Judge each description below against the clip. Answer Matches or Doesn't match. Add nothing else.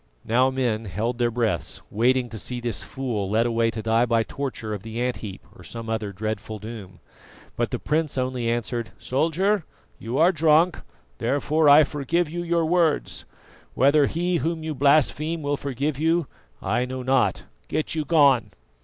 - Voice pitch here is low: Matches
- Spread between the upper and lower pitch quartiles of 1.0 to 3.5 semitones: Doesn't match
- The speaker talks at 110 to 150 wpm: Doesn't match